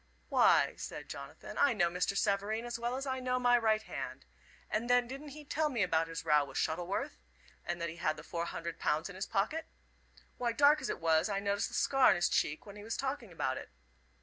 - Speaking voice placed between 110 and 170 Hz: No, high, 205 Hz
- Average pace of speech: No, fast, 230 wpm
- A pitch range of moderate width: No, wide, 6.8 semitones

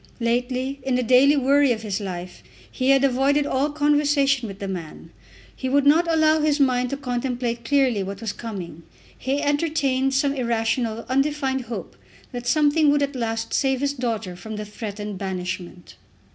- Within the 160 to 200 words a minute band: Yes, average, 170 wpm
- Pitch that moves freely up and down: No, average, 4.0 semitones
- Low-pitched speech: No, very high, 255 Hz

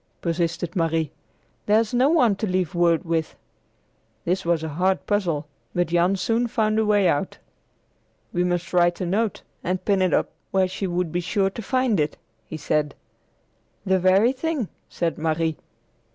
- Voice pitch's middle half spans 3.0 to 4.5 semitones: Yes, average, 3.6 semitones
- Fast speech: No, average, 165 wpm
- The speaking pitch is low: No, medium, 180 Hz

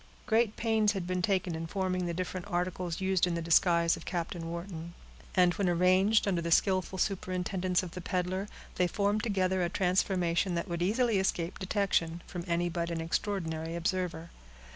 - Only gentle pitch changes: Yes, narrow, 2.0 semitones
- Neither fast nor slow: Yes, average, 175 wpm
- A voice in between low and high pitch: Yes, medium, 180 Hz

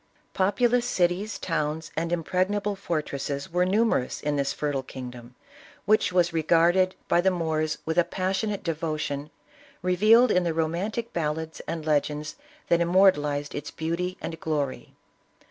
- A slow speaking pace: No, average, 165 wpm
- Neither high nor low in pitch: Yes, medium, 170 Hz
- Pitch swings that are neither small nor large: Yes, average, 3.7 semitones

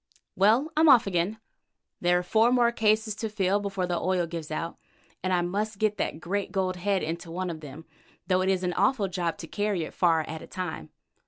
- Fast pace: Yes, fast, 220 wpm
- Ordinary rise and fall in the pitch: Yes, average, 3.3 semitones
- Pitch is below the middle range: No, medium, 185 Hz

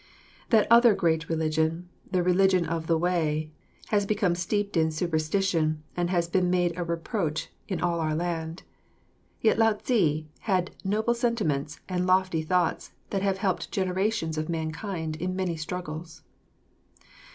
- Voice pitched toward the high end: No, medium, 175 Hz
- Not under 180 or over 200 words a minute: No, average, 145 wpm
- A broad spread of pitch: No, average, 3.2 semitones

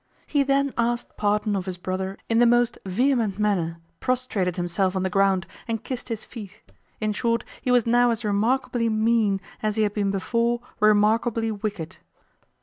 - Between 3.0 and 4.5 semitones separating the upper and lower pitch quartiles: Yes, average, 3.3 semitones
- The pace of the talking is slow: No, average, 170 wpm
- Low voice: No, high, 215 Hz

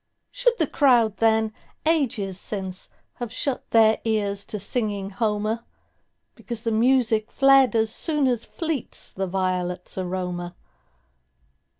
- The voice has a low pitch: No, high, 220 Hz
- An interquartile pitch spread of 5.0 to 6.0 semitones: No, average, 4.3 semitones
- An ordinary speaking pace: No, slow, 105 wpm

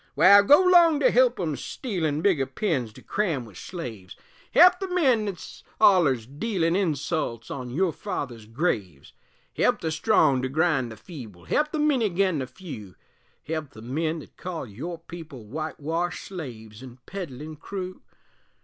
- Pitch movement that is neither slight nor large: No, wide, 7.1 semitones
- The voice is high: No, medium, 160 Hz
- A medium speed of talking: Yes, average, 160 wpm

